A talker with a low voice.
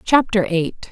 No: high, 200 Hz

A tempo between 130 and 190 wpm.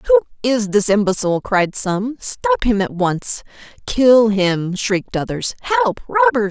Yes: average, 150 wpm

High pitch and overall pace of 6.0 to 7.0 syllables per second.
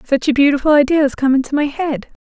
Yes: very high, 280 Hz; 6.4 syllables/s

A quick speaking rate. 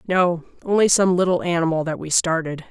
No: average, 175 wpm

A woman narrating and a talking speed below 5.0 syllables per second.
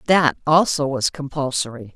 Yes: female; 4.8 syllables/s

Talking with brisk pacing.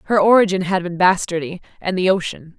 No: average, 185 wpm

